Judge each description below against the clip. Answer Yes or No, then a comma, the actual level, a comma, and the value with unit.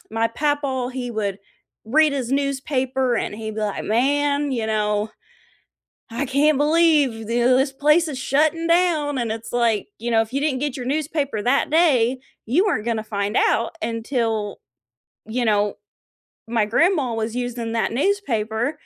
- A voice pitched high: Yes, very high, 250 Hz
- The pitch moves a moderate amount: Yes, average, 4.4 semitones